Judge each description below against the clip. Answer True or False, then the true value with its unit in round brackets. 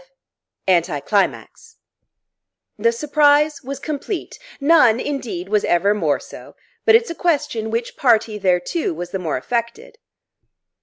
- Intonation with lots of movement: True (7.4 semitones)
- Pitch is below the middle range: False (235 Hz)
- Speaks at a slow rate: True (125 wpm)